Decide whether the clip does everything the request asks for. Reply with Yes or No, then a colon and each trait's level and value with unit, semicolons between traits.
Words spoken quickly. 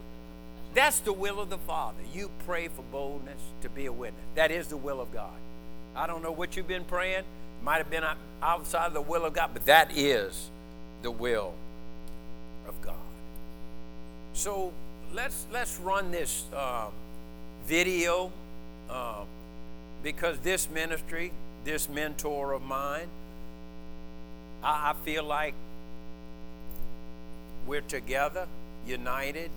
No: slow, 135 wpm